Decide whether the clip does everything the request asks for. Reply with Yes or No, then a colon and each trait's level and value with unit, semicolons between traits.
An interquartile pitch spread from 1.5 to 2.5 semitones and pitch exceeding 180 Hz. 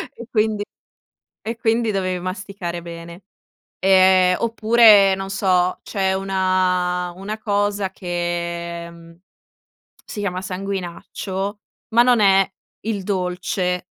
Yes: narrow, 2.2 semitones; high, 190 Hz